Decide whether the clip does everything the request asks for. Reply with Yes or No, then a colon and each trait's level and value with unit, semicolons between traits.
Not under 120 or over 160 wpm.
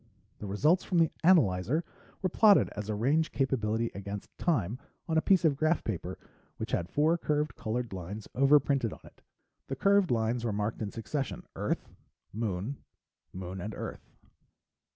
Yes: average, 155 wpm